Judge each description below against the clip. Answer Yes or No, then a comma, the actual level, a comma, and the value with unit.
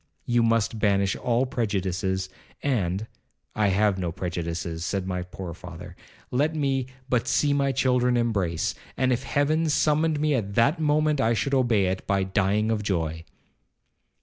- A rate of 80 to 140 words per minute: No, average, 155 wpm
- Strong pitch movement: Yes, wide, 6.1 semitones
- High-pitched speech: No, low, 110 Hz